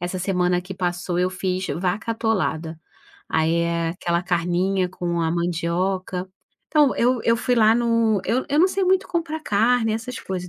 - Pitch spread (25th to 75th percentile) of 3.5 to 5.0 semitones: Yes, average, 4.7 semitones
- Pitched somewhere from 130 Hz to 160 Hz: No, medium, 185 Hz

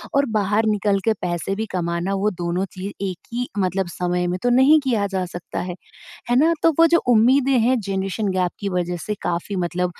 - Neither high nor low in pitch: No, high, 195 Hz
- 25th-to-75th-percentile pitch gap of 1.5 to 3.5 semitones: No, average, 4.3 semitones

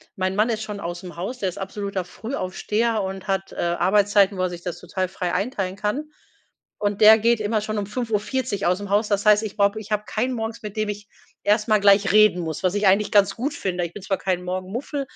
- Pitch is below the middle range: No, high, 205 Hz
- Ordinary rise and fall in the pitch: No, narrow, 2.2 semitones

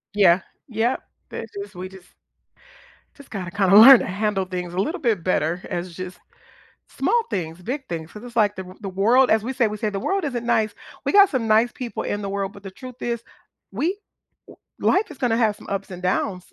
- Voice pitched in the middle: No, high, 210 Hz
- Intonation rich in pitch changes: No, average, 4.5 semitones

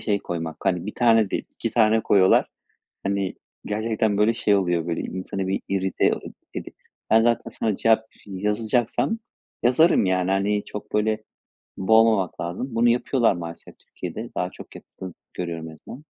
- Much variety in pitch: No, average, 3.2 semitones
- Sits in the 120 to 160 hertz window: No, low, 105 Hz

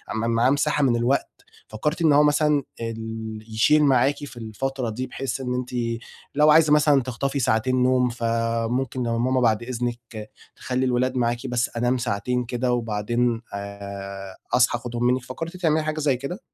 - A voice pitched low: Yes, low, 125 Hz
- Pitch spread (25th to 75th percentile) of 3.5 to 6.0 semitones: No, average, 2.8 semitones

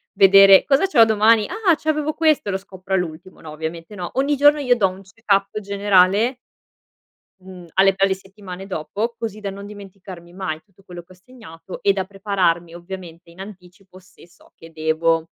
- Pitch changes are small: No, average, 3.0 semitones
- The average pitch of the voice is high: Yes, high, 195 Hz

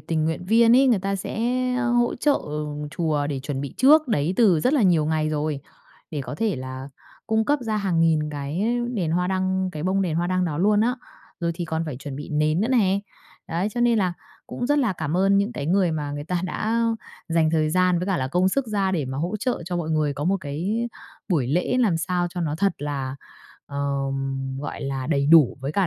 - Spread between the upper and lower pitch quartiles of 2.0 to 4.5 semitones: No, average, 5.2 semitones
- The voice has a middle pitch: Yes, medium, 170 Hz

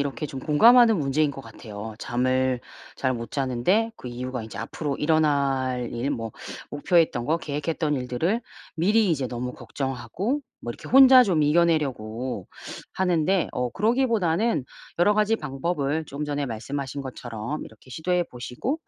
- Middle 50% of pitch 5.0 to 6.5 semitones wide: Yes, wide, 5.6 semitones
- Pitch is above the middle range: No, medium, 145 Hz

